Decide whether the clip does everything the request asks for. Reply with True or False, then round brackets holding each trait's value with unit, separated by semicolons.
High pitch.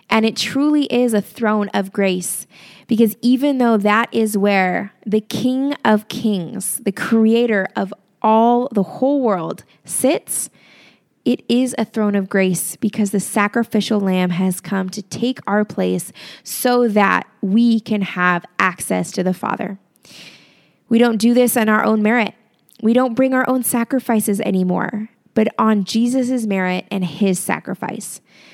True (215 Hz)